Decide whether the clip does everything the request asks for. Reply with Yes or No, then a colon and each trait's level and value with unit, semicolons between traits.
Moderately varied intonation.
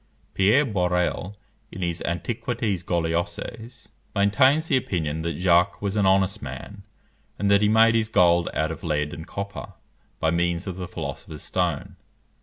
Yes: average, 3.6 semitones